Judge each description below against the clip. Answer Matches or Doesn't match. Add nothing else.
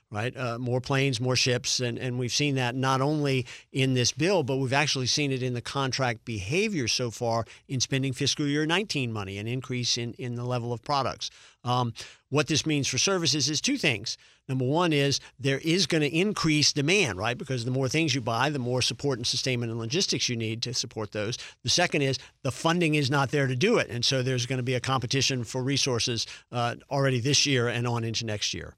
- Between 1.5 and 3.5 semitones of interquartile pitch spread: Matches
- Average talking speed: Doesn't match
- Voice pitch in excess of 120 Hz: Matches